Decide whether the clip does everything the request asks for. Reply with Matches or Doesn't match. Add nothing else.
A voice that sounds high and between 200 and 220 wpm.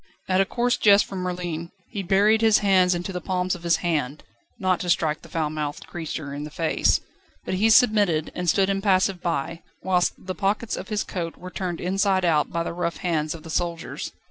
Doesn't match